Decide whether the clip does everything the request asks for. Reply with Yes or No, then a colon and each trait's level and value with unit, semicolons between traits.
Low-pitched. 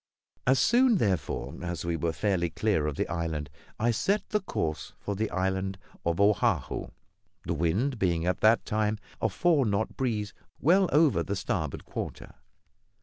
Yes: low, 100 Hz